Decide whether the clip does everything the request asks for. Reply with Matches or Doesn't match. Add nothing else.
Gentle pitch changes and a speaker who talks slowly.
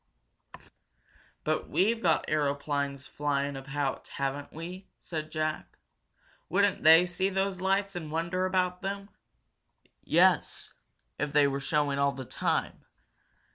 Doesn't match